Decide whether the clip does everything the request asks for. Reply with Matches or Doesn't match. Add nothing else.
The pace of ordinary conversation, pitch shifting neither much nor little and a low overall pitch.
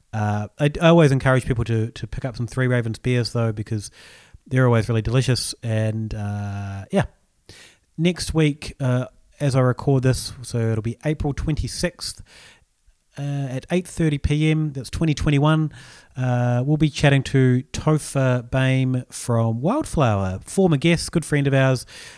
Matches